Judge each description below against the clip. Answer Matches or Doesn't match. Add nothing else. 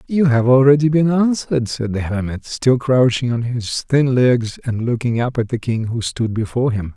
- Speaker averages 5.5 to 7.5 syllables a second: Doesn't match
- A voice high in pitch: Doesn't match